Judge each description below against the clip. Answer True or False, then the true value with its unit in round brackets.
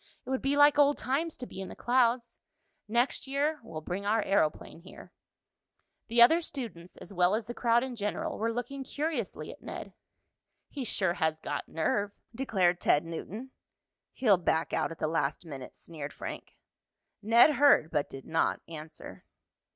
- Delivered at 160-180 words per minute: True (170 wpm)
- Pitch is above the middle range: True (220 Hz)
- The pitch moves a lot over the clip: True (7.7 semitones)